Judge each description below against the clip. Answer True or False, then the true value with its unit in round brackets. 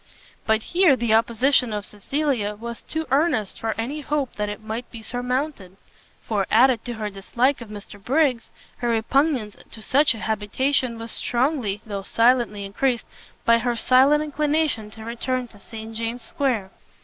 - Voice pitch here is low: False (235 Hz)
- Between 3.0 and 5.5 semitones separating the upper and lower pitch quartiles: True (3.7 semitones)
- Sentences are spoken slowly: False (160 wpm)